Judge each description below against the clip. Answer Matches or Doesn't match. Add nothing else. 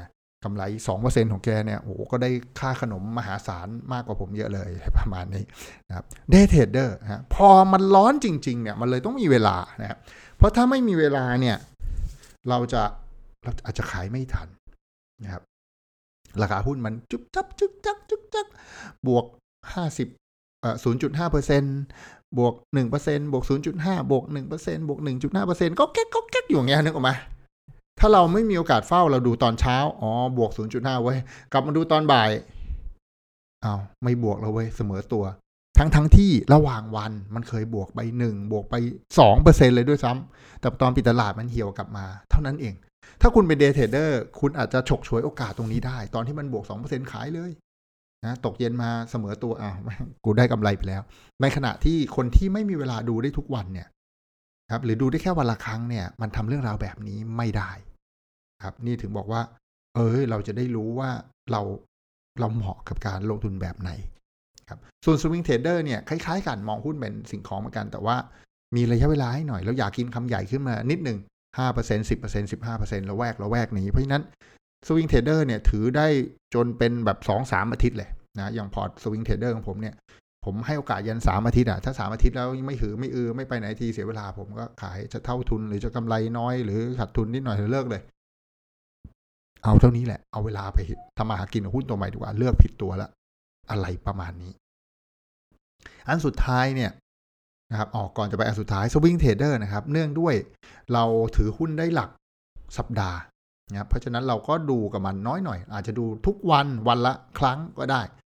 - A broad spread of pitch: Doesn't match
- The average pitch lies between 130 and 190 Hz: Doesn't match